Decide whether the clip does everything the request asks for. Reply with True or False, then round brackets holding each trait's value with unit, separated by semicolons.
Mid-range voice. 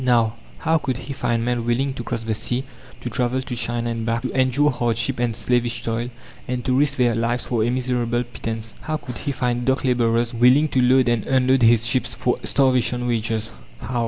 False (120 Hz)